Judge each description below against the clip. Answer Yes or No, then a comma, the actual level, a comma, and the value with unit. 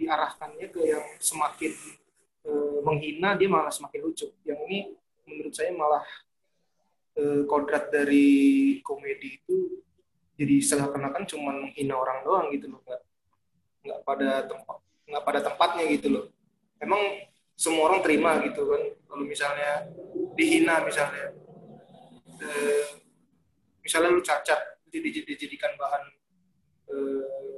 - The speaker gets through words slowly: No, average, 120 wpm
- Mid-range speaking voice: Yes, medium, 165 Hz